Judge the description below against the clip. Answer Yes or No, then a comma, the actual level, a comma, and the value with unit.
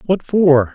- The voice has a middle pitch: Yes, medium, 165 Hz